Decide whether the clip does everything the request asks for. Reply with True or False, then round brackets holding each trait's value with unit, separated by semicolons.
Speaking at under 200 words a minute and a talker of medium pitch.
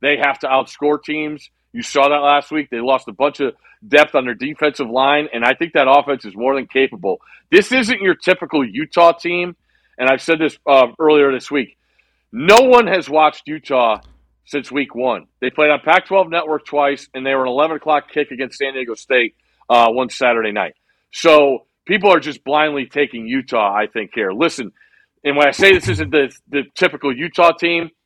False (205 wpm; 145 Hz)